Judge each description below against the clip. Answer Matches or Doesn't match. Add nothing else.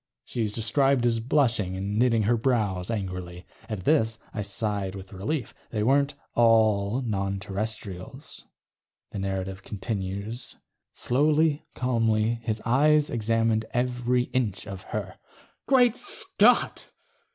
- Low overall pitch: Matches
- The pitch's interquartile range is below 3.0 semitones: Doesn't match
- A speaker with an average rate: Doesn't match